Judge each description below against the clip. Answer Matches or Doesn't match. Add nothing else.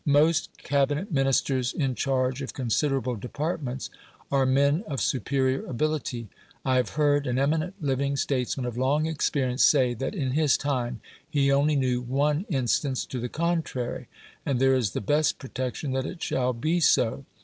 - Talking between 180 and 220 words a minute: Doesn't match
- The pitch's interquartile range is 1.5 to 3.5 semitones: Matches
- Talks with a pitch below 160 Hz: Matches